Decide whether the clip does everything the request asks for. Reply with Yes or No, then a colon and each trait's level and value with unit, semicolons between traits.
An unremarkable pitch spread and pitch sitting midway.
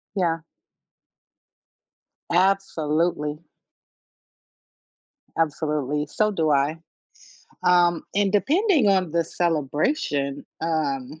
Yes: average, 4.3 semitones; medium, 165 Hz